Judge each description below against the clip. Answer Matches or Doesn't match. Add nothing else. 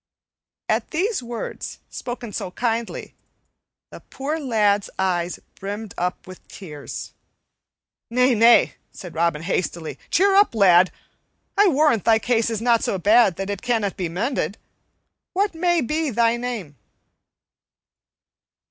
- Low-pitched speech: Doesn't match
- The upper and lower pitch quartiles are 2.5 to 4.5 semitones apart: Doesn't match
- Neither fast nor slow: Doesn't match